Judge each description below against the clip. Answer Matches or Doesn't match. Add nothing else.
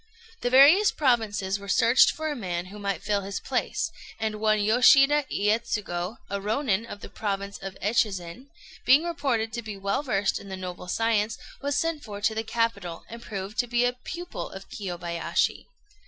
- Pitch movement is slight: Doesn't match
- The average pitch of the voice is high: Matches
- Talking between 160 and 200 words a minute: Matches